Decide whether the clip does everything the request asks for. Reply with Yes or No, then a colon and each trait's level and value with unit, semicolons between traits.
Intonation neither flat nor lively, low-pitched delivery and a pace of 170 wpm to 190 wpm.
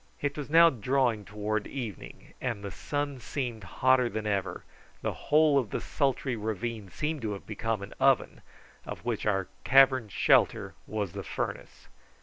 No: average, 4.5 semitones; low, 115 Hz; average, 160 wpm